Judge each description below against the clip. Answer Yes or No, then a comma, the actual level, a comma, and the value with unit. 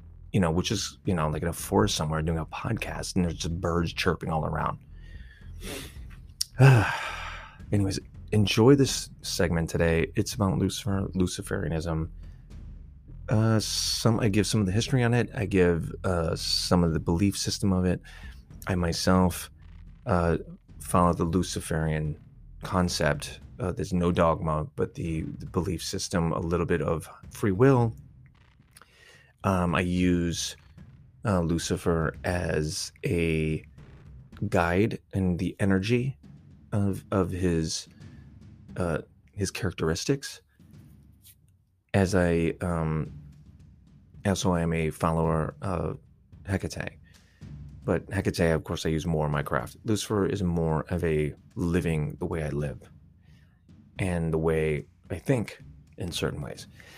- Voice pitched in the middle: No, very low, 85 Hz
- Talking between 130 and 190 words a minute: Yes, slow, 135 wpm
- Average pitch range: Yes, average, 3.3 semitones